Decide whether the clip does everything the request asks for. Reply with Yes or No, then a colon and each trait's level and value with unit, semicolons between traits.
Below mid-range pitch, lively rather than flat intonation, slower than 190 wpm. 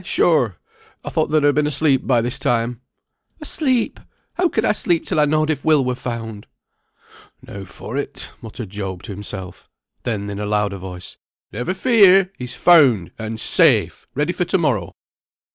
Yes: low, 125 Hz; wide, 7.2 semitones; average, 170 wpm